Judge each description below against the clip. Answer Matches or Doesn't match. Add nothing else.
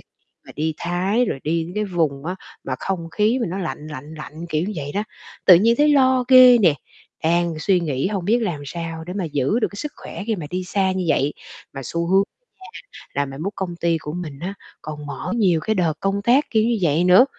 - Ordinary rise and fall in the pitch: Matches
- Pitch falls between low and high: Matches